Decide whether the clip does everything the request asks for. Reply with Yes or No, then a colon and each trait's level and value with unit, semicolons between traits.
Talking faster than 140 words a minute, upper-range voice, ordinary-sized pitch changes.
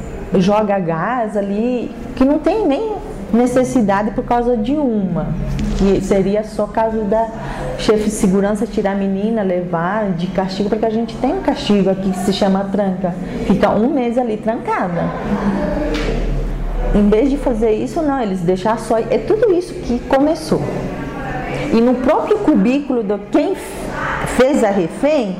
Yes: average, 155 wpm; high, 220 Hz; average, 4.1 semitones